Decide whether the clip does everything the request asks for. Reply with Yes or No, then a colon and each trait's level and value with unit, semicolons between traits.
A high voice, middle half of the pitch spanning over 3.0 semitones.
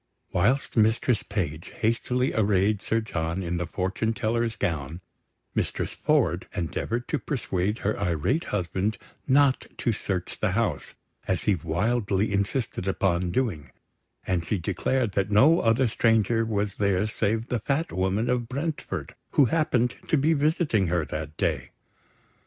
No: low, 105 Hz; average, 4.7 semitones